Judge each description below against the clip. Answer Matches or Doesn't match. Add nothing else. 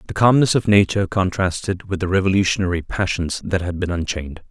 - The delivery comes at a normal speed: Matches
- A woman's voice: Doesn't match